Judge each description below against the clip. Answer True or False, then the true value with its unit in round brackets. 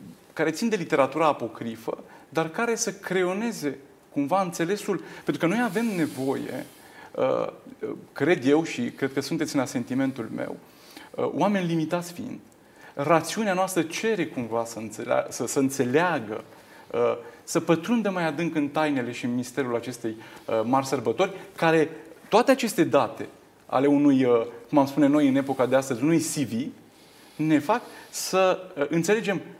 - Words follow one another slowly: False (140 wpm)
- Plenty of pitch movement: True (6.4 semitones)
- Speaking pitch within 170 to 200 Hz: False (160 Hz)